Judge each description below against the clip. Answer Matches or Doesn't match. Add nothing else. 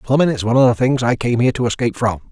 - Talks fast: Matches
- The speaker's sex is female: Doesn't match